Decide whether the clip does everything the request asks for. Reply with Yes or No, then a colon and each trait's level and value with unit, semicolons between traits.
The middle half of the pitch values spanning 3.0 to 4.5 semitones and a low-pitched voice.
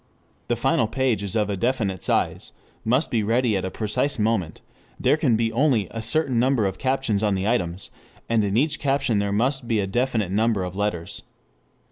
Yes: average, 4.2 semitones; low, 110 Hz